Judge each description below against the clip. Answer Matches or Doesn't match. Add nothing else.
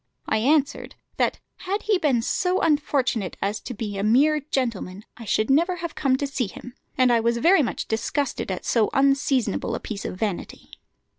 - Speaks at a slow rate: Doesn't match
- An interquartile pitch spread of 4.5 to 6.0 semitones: Matches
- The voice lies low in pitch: Doesn't match